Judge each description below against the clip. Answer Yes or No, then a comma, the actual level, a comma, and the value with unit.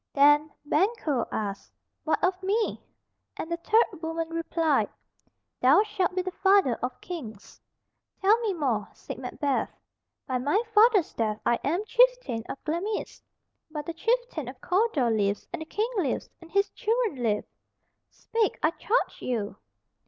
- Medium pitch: No, very high, 330 Hz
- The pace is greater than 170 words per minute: No, average, 150 wpm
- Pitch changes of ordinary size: No, wide, 7.5 semitones